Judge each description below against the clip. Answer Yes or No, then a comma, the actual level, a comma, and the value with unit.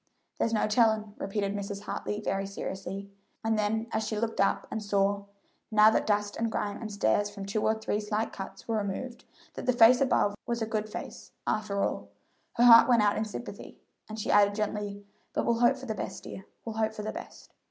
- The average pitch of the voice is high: Yes, high, 210 Hz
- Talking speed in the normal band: No, fast, 215 wpm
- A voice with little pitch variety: Yes, narrow, 1.6 semitones